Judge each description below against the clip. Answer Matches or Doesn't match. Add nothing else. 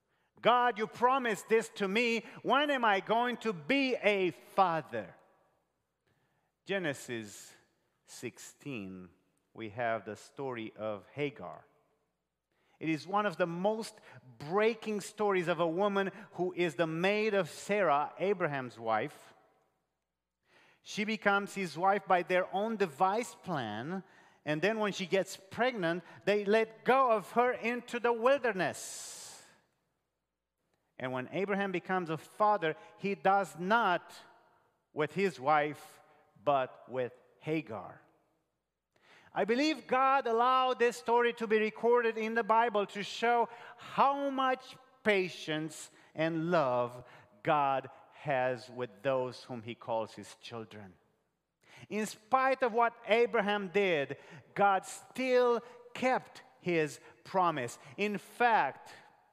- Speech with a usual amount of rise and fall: Doesn't match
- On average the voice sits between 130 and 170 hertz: Doesn't match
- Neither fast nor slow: Doesn't match